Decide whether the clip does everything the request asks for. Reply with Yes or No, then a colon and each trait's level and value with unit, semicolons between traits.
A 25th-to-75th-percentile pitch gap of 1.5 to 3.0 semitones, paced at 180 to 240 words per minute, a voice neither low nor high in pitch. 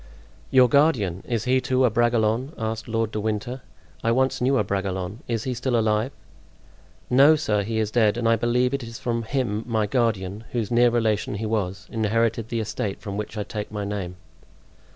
No: narrow, 2.6 semitones; average, 190 wpm; low, 115 Hz